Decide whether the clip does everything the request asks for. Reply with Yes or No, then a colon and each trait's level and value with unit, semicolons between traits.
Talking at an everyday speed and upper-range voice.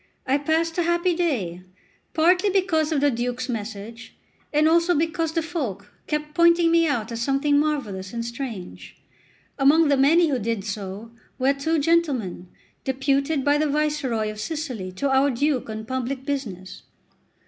Yes: average, 160 wpm; very high, 275 Hz